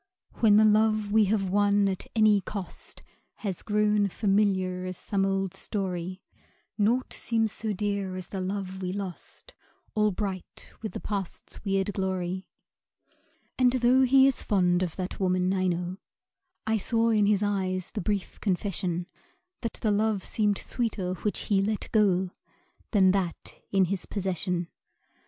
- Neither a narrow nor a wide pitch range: No, narrow, 2.2 semitones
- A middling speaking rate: Yes, average, 150 wpm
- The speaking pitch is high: Yes, high, 200 Hz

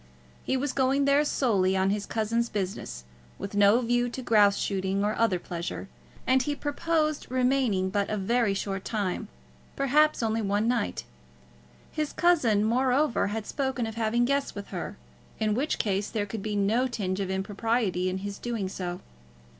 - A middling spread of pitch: Yes, average, 4.5 semitones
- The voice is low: No, high, 220 Hz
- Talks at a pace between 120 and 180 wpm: Yes, average, 170 wpm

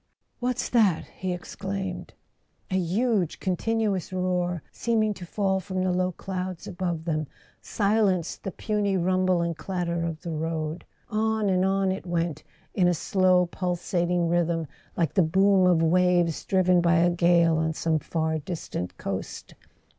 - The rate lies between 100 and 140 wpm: No, average, 155 wpm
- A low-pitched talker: No, medium, 180 Hz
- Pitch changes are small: Yes, narrow, 2.3 semitones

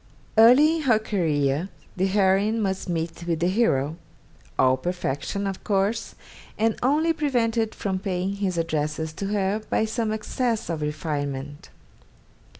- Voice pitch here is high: Yes, high, 195 Hz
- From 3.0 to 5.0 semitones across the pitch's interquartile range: No, wide, 5.6 semitones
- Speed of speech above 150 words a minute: No, average, 140 wpm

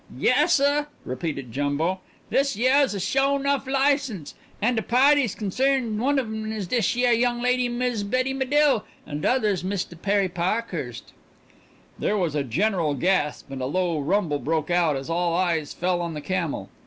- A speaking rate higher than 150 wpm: Yes, average, 170 wpm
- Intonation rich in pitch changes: Yes, wide, 7.2 semitones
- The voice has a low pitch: No, high, 200 Hz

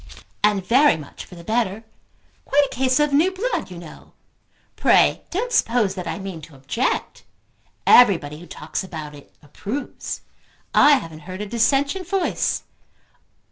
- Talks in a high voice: Yes, high, 210 Hz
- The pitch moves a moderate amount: No, wide, 8.8 semitones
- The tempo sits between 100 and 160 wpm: Yes, average, 150 wpm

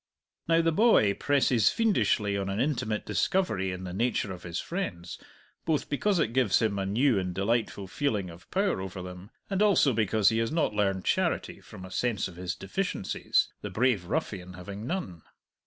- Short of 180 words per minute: No, average, 185 wpm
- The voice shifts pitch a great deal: Yes, wide, 7.2 semitones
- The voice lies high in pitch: No, low, 105 Hz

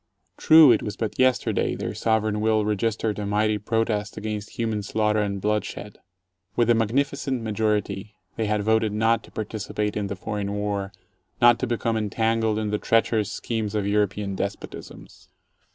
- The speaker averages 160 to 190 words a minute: Yes, average, 165 wpm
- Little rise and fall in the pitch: Yes, narrow, 1.4 semitones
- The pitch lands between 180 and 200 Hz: No, low, 105 Hz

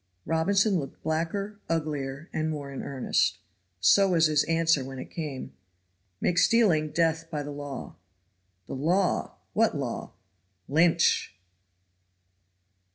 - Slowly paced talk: Yes, slow, 120 wpm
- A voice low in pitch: No, medium, 160 Hz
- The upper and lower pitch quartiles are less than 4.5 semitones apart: Yes, average, 3.0 semitones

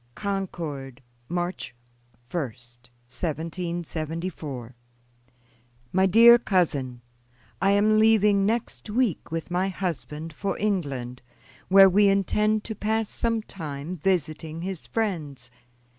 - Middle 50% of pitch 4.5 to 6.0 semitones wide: Yes, wide, 5.4 semitones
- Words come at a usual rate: No, slow, 100 wpm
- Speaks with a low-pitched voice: No, medium, 180 Hz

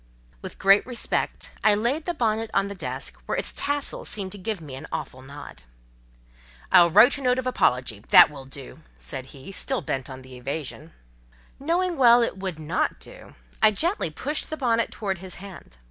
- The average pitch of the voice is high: Yes, high, 195 Hz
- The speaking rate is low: No, average, 180 wpm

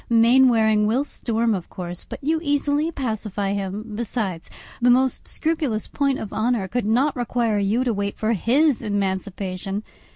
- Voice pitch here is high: Yes, high, 225 Hz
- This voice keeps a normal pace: Yes, average, 155 wpm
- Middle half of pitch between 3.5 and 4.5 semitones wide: Yes, average, 4.2 semitones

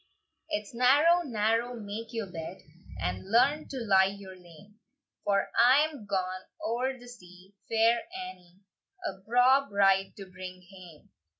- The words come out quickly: No, average, 140 wpm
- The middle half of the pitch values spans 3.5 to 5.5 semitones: Yes, average, 4.7 semitones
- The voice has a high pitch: Yes, high, 210 Hz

